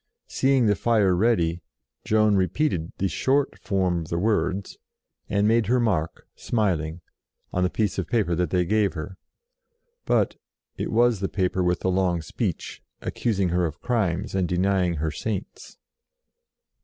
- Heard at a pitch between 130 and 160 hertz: No, very low, 95 Hz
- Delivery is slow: No, average, 150 wpm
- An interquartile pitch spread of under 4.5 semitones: Yes, average, 3.7 semitones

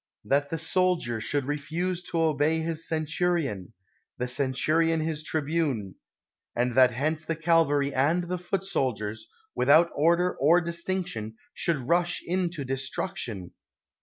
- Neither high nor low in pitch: Yes, medium, 155 Hz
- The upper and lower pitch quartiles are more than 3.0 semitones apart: Yes, average, 4.3 semitones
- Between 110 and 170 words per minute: Yes, slow, 135 wpm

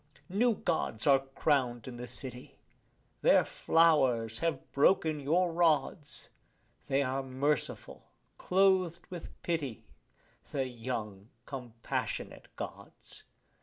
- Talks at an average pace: No, slow, 100 wpm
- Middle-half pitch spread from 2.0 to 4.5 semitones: No, average, 5.1 semitones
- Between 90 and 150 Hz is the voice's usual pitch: Yes, medium, 140 Hz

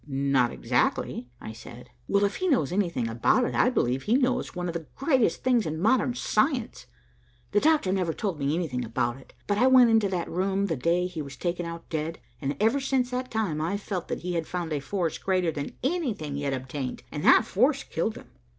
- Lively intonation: Yes, wide, 7.5 semitones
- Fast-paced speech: Yes, fast, 220 wpm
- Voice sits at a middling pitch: Yes, medium, 175 Hz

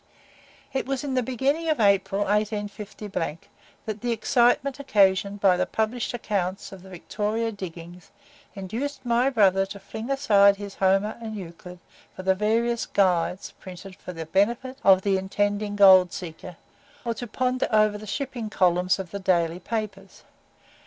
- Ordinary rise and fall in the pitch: Yes, average, 3.5 semitones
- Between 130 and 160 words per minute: Yes, average, 155 wpm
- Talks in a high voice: Yes, high, 205 Hz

